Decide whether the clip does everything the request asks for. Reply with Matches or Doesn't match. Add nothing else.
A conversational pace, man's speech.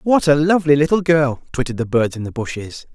Doesn't match